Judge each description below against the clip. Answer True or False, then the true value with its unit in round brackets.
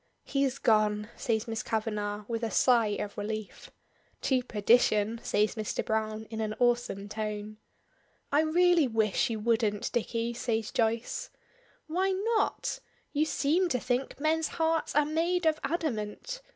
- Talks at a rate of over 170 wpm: False (140 wpm)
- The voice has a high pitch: True (230 Hz)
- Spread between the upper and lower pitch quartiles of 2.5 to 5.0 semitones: False (5.5 semitones)